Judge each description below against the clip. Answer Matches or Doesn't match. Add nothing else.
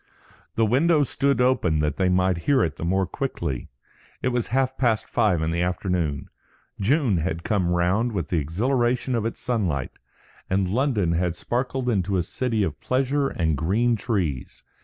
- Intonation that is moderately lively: Doesn't match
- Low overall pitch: Matches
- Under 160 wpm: Doesn't match